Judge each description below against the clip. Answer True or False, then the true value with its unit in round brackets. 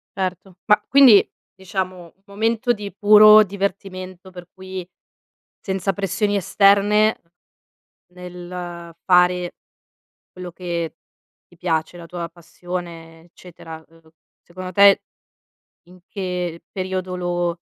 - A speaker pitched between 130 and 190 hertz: True (185 Hz)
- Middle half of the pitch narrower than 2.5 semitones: True (2.1 semitones)